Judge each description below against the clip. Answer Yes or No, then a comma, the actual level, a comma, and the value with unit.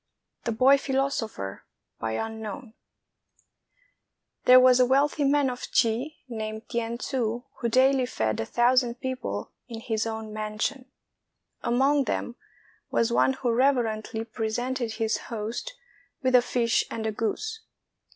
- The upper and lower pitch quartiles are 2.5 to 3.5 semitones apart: Yes, average, 2.9 semitones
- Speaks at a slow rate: Yes, slow, 125 wpm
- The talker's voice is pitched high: Yes, high, 240 Hz